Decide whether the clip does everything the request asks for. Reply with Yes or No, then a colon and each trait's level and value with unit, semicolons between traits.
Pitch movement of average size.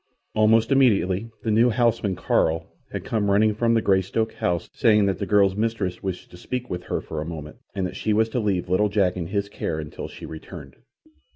Yes: average, 3.7 semitones